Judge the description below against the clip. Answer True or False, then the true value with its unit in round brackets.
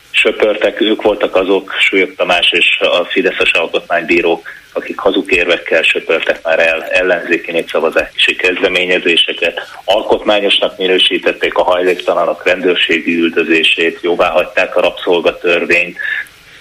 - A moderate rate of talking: False (100 wpm)